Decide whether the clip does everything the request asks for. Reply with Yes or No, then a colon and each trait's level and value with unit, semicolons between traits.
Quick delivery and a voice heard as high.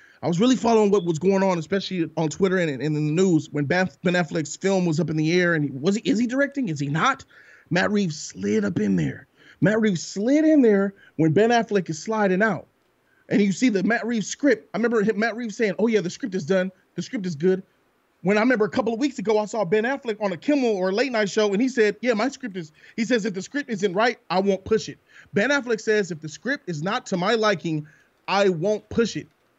Yes: fast, 255 wpm; high, 200 Hz